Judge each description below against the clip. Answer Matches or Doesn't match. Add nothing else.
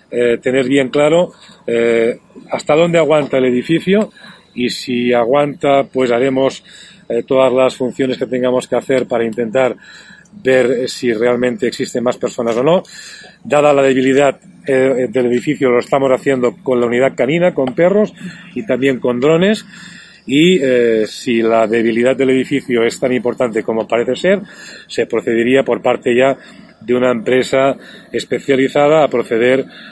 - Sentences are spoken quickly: Doesn't match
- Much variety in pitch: Doesn't match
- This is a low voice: Matches